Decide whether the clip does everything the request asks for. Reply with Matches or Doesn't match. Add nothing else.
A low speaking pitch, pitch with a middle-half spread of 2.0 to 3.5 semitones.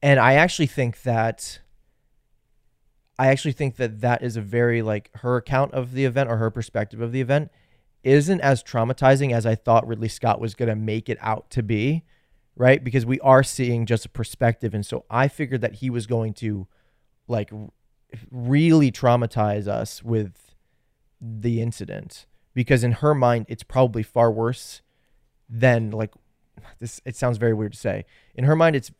Matches